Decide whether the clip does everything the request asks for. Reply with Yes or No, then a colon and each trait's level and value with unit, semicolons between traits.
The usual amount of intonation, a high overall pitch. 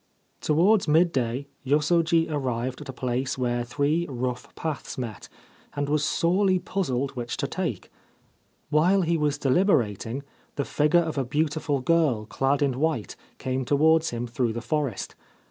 No: average, 4.3 semitones; medium, 145 Hz